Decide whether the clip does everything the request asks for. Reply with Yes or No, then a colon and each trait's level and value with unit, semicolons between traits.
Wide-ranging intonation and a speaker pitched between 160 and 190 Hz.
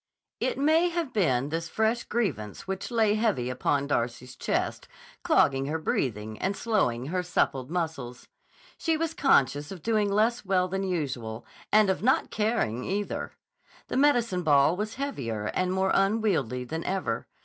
Yes: wide, 8.7 semitones; medium, 185 Hz